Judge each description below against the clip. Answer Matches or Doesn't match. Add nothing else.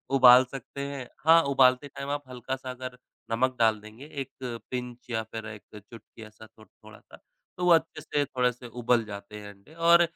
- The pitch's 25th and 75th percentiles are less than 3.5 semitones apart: Doesn't match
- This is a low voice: Matches